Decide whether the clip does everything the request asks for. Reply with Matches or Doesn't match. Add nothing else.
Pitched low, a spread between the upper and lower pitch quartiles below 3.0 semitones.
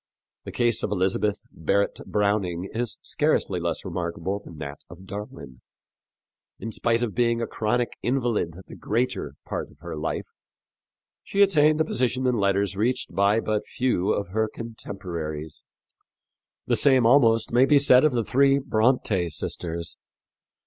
Doesn't match